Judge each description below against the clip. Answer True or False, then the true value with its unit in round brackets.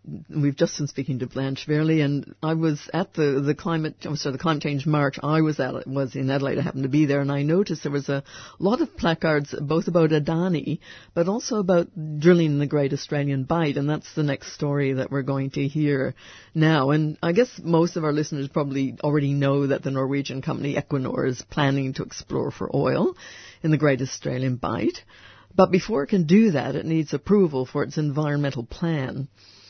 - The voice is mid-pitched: True (145 Hz)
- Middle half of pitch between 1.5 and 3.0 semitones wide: True (2.6 semitones)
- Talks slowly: False (205 wpm)